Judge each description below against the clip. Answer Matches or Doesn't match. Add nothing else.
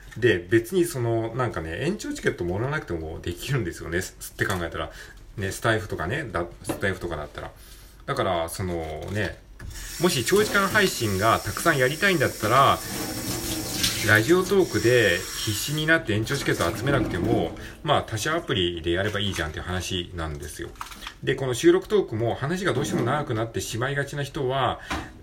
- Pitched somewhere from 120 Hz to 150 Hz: Doesn't match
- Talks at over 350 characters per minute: Matches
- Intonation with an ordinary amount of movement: Doesn't match